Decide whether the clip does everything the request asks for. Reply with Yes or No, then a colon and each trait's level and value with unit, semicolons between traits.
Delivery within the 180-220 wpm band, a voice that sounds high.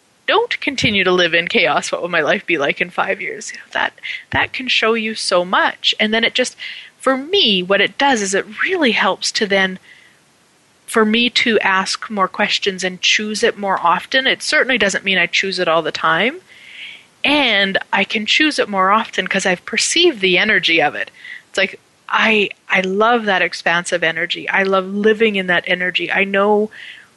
Yes: average, 200 wpm; high, 200 Hz